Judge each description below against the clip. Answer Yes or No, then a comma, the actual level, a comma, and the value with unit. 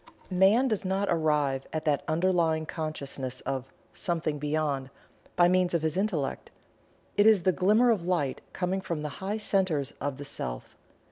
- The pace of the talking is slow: No, average, 160 wpm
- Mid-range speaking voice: Yes, medium, 165 Hz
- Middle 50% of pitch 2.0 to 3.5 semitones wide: No, average, 4.7 semitones